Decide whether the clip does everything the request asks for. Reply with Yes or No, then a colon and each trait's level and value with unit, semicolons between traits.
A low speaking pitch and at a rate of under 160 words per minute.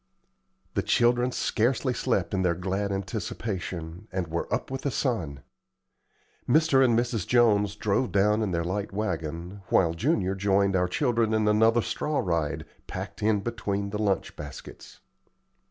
Yes: low, 100 Hz; average, 150 wpm